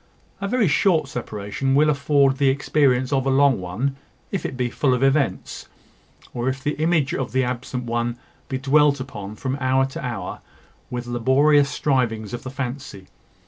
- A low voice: Yes, low, 130 Hz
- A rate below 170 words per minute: No, average, 175 wpm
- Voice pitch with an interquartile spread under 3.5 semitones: Yes, narrow, 2.5 semitones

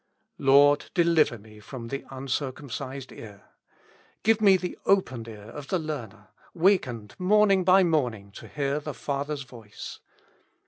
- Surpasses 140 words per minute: No, slow, 135 wpm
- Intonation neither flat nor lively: No, wide, 6.5 semitones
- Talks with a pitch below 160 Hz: Yes, medium, 140 Hz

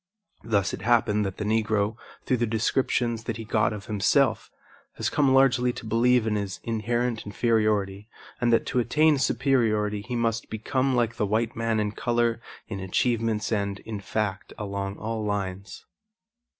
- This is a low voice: Yes, low, 110 Hz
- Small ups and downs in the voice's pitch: Yes, narrow, 2.2 semitones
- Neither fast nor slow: Yes, average, 165 wpm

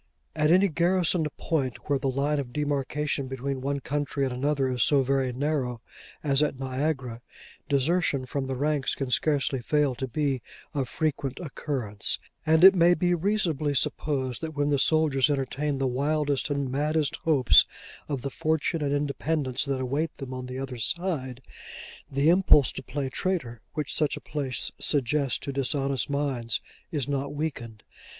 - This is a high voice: No, medium, 140 Hz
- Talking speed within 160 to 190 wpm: Yes, average, 165 wpm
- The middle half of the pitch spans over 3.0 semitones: No, narrow, 2.5 semitones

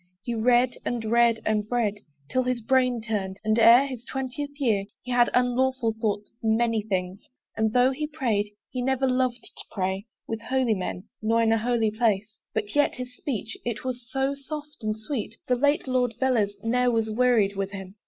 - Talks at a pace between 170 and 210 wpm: Yes, average, 195 wpm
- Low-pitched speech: No, high, 235 Hz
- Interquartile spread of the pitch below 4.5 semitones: Yes, average, 2.8 semitones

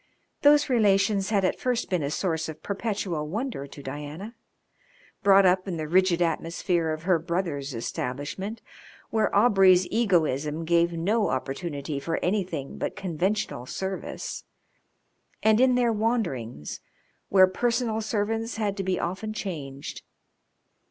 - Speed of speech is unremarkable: No, slow, 130 wpm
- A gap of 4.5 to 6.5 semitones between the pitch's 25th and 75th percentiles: Yes, average, 5.3 semitones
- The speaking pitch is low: No, medium, 185 Hz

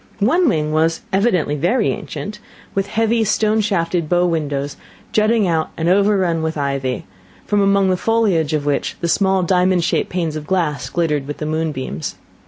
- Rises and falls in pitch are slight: No, average, 4.7 semitones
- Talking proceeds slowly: No, average, 170 wpm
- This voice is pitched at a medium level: Yes, medium, 175 Hz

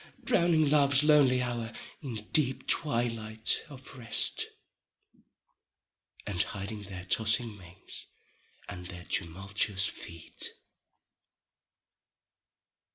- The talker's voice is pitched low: Yes, low, 110 Hz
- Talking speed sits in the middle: No, slow, 85 wpm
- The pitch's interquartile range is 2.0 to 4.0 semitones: No, wide, 5.5 semitones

